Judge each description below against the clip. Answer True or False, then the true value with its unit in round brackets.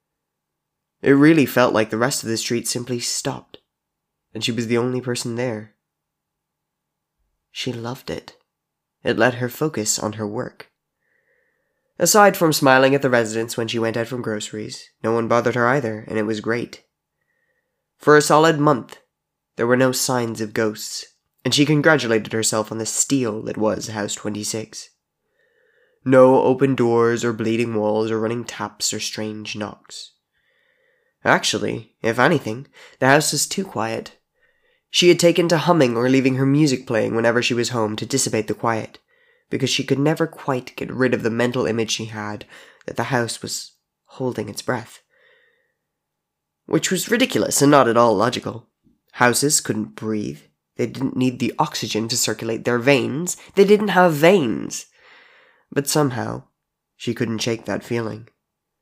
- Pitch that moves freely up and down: False (5.0 semitones)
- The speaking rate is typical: True (160 wpm)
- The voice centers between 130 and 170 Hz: False (120 Hz)